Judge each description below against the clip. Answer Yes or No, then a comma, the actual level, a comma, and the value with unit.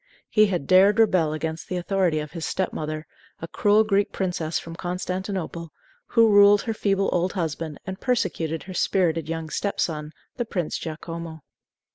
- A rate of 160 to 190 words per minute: Yes, average, 165 wpm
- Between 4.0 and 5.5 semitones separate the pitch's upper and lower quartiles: No, average, 3.6 semitones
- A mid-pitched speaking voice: Yes, medium, 180 Hz